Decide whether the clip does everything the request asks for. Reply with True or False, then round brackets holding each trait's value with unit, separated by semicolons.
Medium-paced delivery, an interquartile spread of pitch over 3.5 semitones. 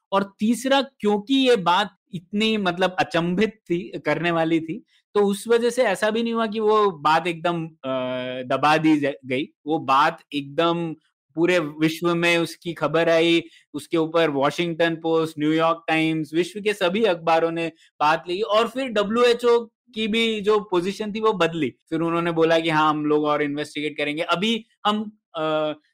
True (170 wpm; 5.1 semitones)